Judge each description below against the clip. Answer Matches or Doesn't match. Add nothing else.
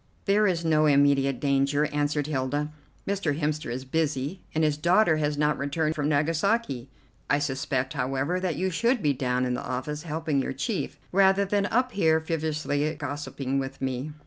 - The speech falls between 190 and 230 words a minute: Doesn't match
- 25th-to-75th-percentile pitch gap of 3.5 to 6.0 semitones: Doesn't match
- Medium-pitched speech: Matches